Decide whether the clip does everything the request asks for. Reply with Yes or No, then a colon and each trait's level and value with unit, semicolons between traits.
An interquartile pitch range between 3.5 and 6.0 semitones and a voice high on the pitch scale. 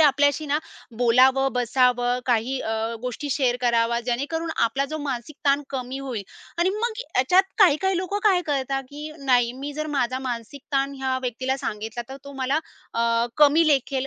No: average, 3.1 semitones; very high, 270 Hz